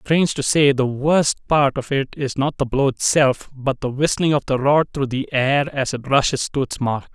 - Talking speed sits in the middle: No, fast, 235 wpm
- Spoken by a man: Yes, male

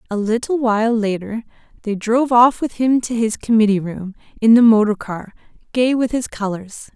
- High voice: Yes, high, 225 Hz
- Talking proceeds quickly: No, average, 180 wpm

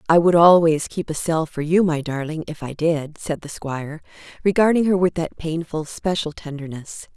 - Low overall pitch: No, medium, 160 Hz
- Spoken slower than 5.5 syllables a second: Yes, 5.0 syllables/s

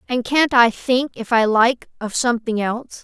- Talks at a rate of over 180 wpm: Yes, average, 200 wpm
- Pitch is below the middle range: No, high, 240 Hz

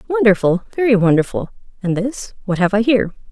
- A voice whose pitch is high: Yes, high, 215 Hz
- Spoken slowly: Yes, slow, 125 wpm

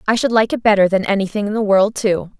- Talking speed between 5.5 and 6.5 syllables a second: Yes, 6.4 syllables/s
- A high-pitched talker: Yes, high, 205 Hz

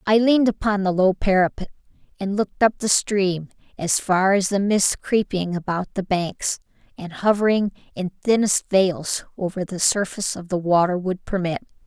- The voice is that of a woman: Yes, female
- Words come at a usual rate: Yes, average, 165 wpm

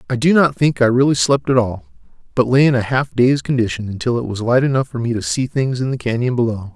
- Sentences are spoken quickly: Yes, fast, 265 wpm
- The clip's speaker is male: Yes, male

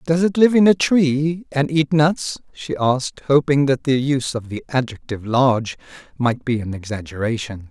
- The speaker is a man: Yes, male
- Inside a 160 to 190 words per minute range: Yes, average, 180 wpm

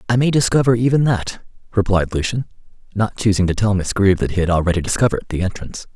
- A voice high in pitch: No, low, 105 Hz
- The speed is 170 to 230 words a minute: Yes, average, 200 wpm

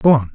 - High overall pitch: No, low, 125 Hz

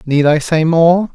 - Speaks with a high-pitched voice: No, medium, 160 Hz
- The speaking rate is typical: No, fast, 210 wpm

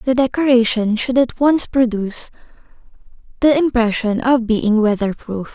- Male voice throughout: No, female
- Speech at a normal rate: No, slow, 130 wpm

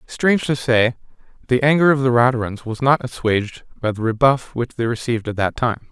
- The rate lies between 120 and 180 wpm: No, fast, 205 wpm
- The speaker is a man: Yes, male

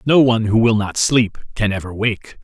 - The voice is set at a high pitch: No, low, 110 Hz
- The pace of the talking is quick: Yes, fast, 220 wpm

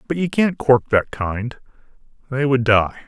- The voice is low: Yes, low, 130 Hz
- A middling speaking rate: Yes, average, 175 wpm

